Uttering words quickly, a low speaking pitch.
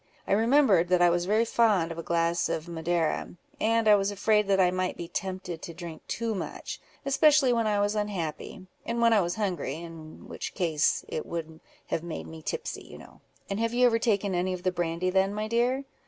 No: fast, 215 wpm; high, 190 Hz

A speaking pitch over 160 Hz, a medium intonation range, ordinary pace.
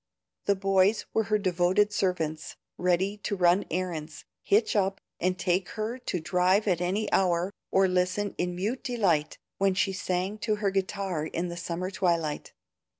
No: medium, 185 Hz; narrow, 2.3 semitones; average, 160 wpm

